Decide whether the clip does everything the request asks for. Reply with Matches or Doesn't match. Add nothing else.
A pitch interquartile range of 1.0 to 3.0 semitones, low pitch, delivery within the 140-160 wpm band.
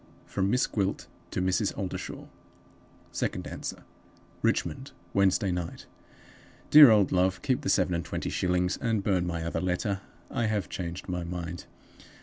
Matches